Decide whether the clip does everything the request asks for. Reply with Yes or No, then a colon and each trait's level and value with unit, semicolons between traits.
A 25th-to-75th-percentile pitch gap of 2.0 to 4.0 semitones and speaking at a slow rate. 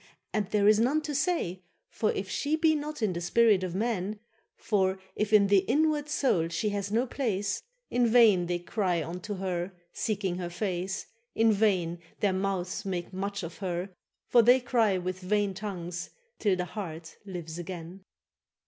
No: average, 3.5 semitones; average, 175 wpm